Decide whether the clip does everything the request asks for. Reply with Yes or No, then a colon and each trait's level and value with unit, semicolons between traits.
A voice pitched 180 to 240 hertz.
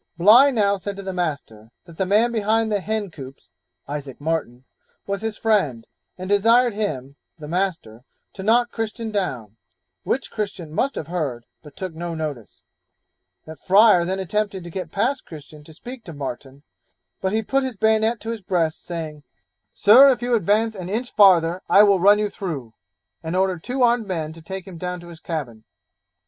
Yes: high, 190 Hz